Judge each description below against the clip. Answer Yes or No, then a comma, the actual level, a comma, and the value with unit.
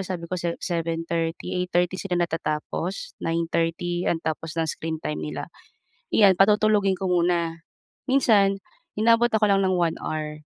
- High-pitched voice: No, medium, 175 Hz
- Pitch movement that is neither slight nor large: Yes, average, 3.0 semitones